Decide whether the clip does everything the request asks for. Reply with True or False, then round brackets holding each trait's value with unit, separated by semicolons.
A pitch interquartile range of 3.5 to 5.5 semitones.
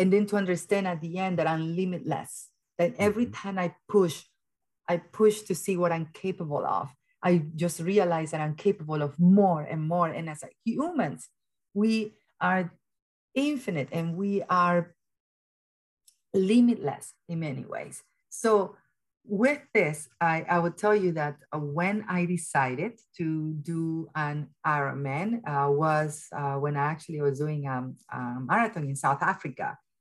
True (4.6 semitones)